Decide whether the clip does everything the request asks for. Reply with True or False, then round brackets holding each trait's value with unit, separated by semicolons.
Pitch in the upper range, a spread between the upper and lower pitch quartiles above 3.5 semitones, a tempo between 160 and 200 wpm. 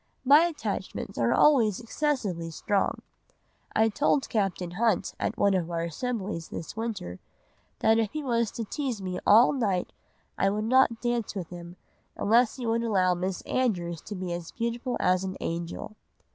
True (215 Hz; 4.7 semitones; 165 wpm)